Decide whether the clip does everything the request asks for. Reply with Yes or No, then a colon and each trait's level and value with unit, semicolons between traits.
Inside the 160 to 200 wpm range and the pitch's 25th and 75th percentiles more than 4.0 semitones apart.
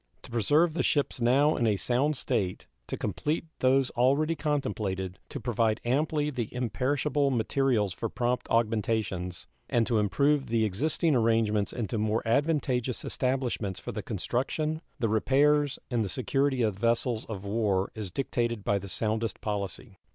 No: average, 150 wpm; average, 4.4 semitones